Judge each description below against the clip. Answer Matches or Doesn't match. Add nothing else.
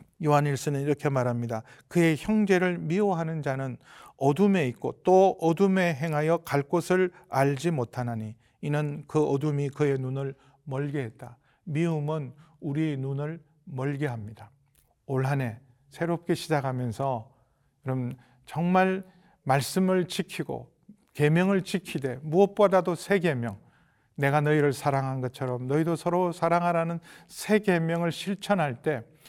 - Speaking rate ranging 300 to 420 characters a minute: Doesn't match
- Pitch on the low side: Doesn't match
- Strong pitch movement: Doesn't match